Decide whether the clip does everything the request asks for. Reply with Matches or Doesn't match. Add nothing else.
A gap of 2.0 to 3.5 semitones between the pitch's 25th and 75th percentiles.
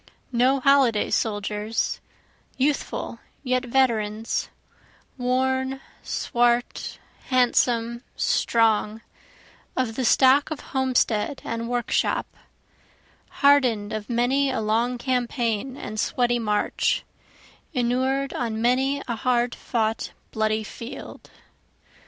Matches